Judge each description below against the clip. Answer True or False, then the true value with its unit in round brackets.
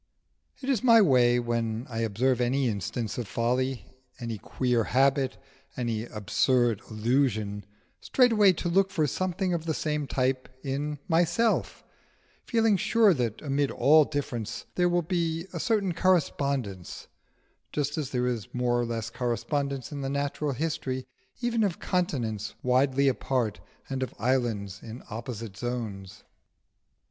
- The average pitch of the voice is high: False (130 Hz)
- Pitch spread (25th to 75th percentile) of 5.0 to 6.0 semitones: True (5.3 semitones)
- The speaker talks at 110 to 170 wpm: True (140 wpm)